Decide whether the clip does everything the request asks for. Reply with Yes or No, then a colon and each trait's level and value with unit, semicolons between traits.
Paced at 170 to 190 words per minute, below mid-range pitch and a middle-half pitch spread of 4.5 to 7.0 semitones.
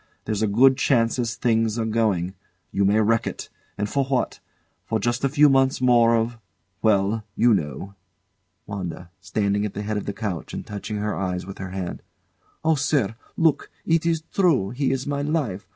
Yes: average, 185 wpm; low, 110 Hz; average, 4.8 semitones